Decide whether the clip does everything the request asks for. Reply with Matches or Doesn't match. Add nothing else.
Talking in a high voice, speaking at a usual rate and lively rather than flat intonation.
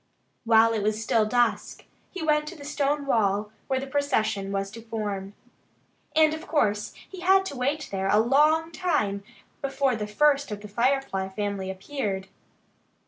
Matches